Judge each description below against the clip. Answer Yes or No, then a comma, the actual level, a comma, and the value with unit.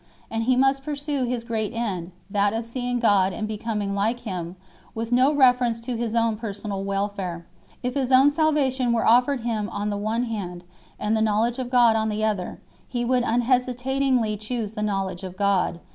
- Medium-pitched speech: No, high, 225 Hz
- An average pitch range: Yes, average, 3.3 semitones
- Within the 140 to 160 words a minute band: No, average, 190 wpm